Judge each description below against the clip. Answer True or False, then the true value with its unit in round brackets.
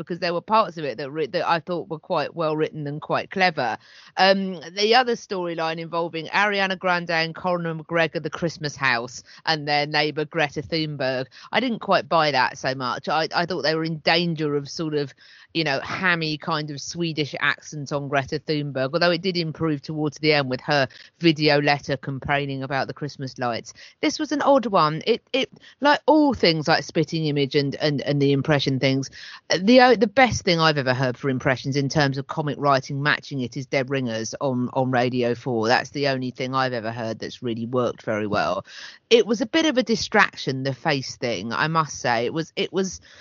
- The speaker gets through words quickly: True (210 wpm)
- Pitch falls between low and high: True (150 Hz)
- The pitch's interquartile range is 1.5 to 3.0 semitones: False (3.9 semitones)